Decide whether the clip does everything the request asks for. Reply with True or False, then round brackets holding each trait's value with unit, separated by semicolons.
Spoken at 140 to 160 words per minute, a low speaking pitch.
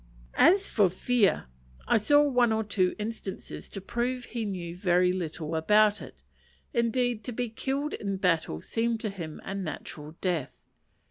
False (155 wpm; 210 Hz)